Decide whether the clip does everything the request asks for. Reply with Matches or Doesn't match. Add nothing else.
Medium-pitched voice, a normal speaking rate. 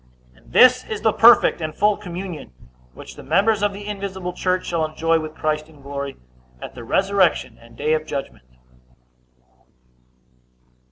Matches